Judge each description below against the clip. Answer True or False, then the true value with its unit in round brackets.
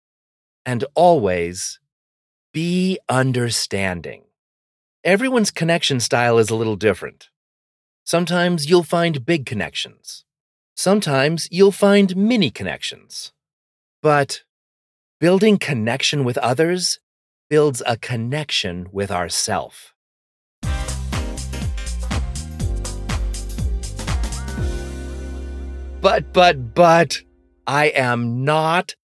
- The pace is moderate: False (75 wpm)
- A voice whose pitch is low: True (115 Hz)